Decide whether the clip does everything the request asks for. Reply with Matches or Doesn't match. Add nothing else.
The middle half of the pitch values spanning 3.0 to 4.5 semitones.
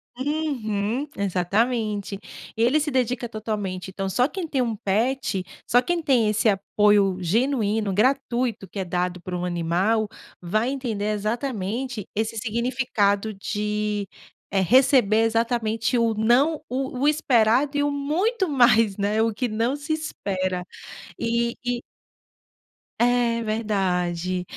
Matches